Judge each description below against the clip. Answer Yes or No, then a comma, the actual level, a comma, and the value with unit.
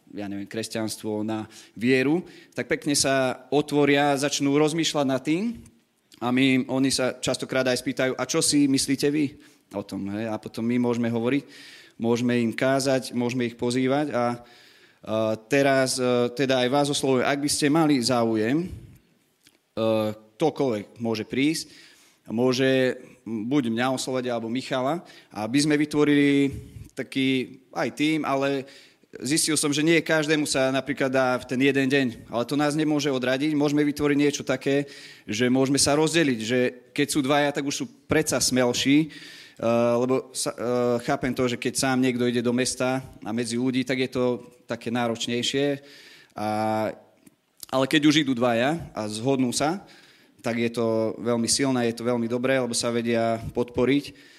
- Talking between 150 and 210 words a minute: Yes, average, 160 wpm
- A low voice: Yes, low, 130 Hz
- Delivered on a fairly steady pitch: No, average, 3.1 semitones